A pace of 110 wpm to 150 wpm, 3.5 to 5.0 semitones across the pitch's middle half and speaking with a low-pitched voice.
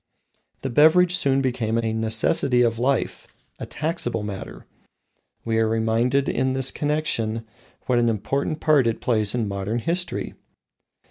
Yes: average, 140 wpm; average, 3.8 semitones; low, 120 Hz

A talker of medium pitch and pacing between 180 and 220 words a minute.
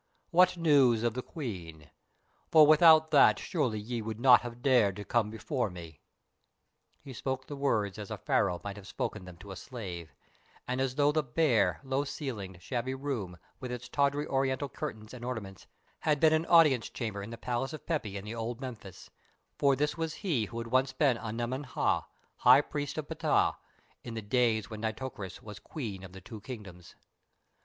No: low, 120 Hz; average, 185 wpm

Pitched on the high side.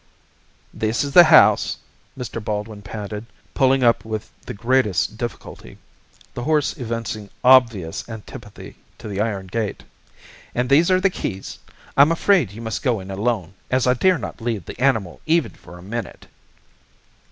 No: low, 115 Hz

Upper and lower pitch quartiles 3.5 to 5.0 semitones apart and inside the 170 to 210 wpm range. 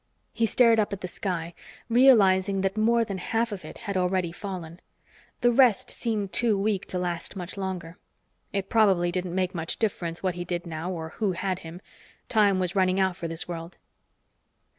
No: average, 3.0 semitones; average, 185 wpm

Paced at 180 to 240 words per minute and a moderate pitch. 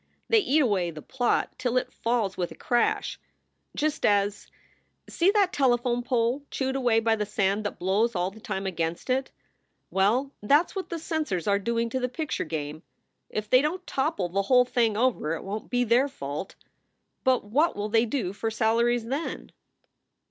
No: average, 190 wpm; high, 235 Hz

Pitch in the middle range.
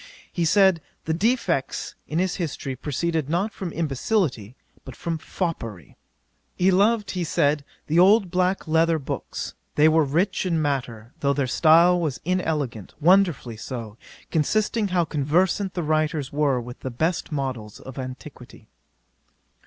Yes: medium, 160 Hz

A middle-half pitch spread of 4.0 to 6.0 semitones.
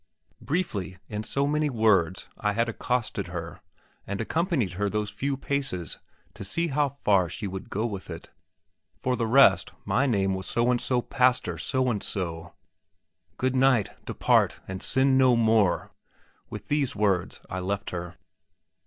Yes: wide, 5.5 semitones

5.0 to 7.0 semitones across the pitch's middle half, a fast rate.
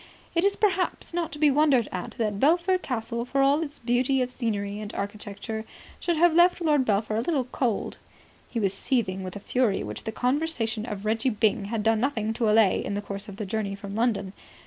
Yes: average, 5.3 semitones; fast, 215 wpm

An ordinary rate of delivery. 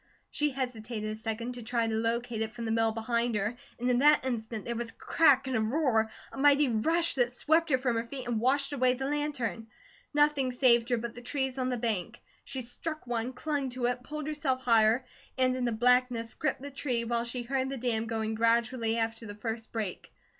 No: fast, 220 wpm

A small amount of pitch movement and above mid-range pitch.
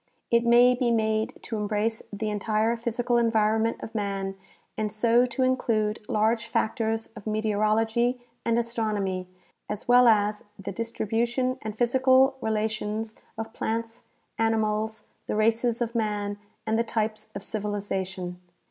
Yes: narrow, 1.7 semitones; high, 220 Hz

